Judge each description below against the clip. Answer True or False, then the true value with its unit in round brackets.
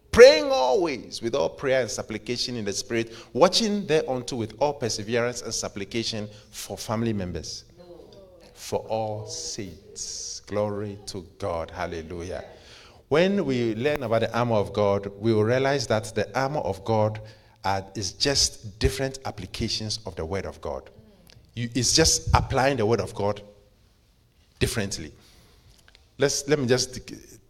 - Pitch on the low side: True (110 Hz)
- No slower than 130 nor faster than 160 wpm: True (145 wpm)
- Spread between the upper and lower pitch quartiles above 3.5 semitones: True (3.9 semitones)